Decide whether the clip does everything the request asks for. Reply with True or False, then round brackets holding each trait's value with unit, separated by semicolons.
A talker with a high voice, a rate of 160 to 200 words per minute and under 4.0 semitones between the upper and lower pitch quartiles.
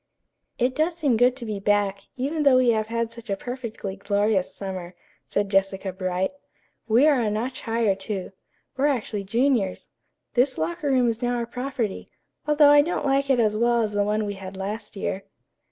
False (225 Hz; 190 wpm; 4.4 semitones)